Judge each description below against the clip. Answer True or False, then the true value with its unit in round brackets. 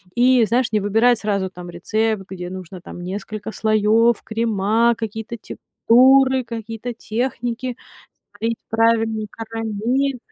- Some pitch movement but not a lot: False (2.1 semitones)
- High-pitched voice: True (225 Hz)